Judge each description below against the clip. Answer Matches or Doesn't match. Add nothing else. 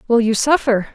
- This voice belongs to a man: Doesn't match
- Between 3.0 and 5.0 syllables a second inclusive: Doesn't match